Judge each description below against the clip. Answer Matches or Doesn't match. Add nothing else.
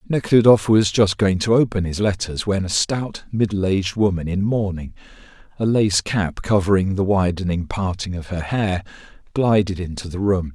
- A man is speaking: Matches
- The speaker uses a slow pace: Doesn't match